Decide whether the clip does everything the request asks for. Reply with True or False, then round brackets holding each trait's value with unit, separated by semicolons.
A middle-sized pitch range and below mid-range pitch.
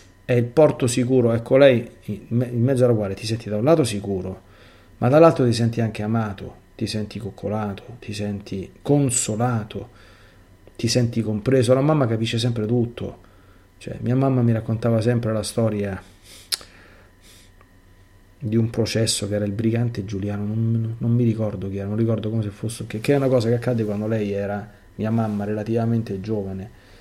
True (3.0 semitones; 110 Hz)